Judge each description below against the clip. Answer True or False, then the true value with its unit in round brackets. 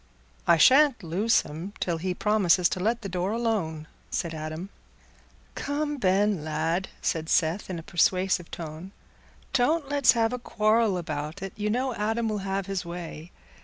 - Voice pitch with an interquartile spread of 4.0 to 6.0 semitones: True (4.9 semitones)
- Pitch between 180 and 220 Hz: True (190 Hz)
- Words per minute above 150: True (165 wpm)